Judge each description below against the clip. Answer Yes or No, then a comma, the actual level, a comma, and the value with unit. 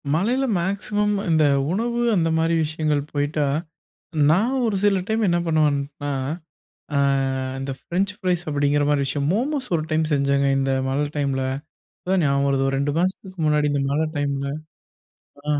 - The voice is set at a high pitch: No, medium, 155 Hz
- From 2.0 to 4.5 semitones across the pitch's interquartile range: No, average, 5.0 semitones